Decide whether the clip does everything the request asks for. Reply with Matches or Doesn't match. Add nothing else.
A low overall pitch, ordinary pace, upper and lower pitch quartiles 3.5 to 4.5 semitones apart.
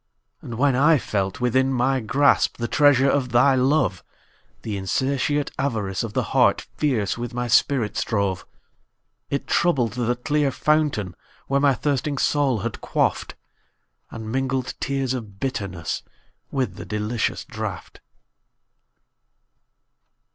Doesn't match